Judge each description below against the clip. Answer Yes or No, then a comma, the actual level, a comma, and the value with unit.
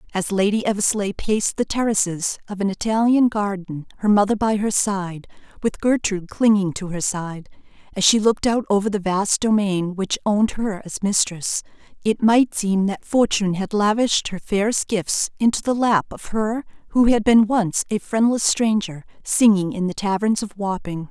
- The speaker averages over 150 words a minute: Yes, average, 175 wpm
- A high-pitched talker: Yes, high, 205 Hz